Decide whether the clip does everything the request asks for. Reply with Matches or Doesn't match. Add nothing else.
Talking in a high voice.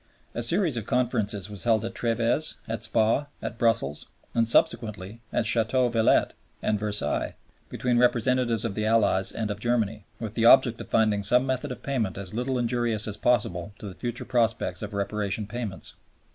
Doesn't match